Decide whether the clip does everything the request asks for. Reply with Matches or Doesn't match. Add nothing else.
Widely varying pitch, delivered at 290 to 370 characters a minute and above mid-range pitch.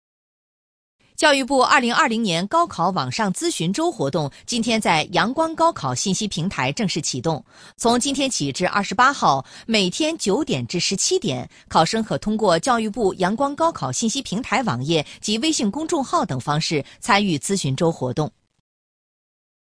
Doesn't match